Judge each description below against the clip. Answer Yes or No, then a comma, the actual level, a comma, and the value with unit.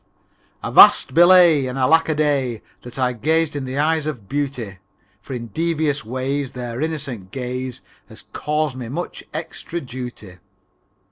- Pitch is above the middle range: No, low, 135 Hz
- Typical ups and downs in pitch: Yes, average, 3.8 semitones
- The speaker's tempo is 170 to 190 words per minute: No, average, 150 wpm